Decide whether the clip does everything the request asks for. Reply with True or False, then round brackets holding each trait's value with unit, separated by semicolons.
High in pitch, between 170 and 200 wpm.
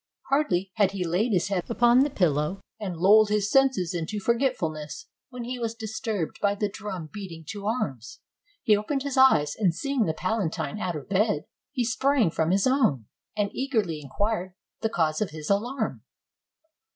True (205 Hz; 175 wpm)